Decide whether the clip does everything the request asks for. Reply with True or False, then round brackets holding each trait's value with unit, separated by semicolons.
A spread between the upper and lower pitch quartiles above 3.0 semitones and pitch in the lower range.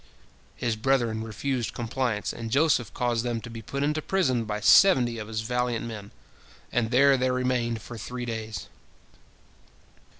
False (2.4 semitones; 120 Hz)